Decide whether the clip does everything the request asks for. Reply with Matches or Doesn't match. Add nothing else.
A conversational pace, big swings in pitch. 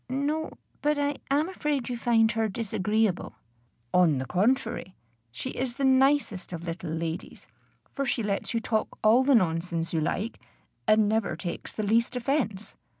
Matches